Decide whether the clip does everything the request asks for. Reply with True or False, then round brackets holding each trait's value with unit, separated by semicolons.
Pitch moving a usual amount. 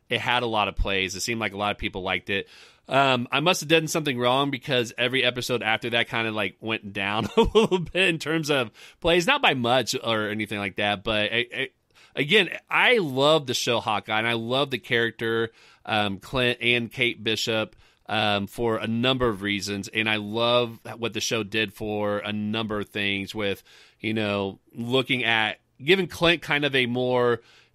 True (3.2 semitones)